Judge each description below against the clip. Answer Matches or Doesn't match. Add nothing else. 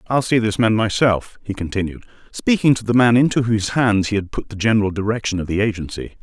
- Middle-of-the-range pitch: Doesn't match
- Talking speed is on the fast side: Matches